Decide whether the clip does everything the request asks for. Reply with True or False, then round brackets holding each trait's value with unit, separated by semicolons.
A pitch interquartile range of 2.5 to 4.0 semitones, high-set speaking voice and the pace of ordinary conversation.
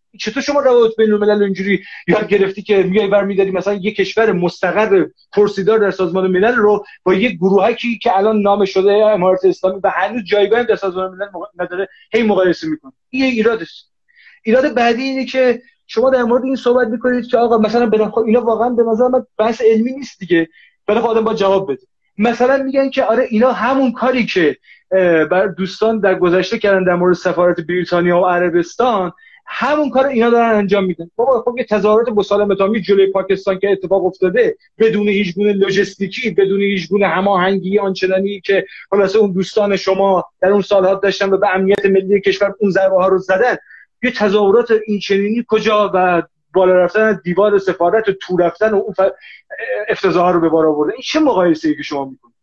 False (3.4 semitones; 200 Hz; 185 wpm)